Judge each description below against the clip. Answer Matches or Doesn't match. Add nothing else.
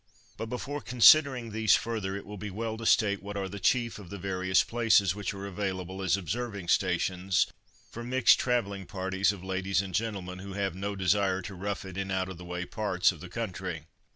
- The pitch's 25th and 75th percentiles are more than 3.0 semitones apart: Doesn't match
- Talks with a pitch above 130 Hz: Doesn't match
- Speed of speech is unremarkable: Doesn't match